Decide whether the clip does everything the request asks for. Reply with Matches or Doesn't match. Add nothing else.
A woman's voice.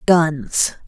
Matches